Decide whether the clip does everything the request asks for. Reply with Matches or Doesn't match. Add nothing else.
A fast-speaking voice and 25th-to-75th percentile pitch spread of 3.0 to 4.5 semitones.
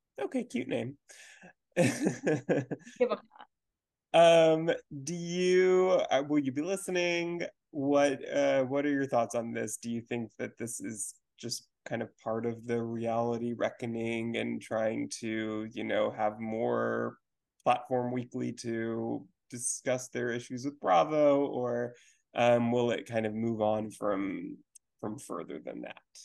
Doesn't match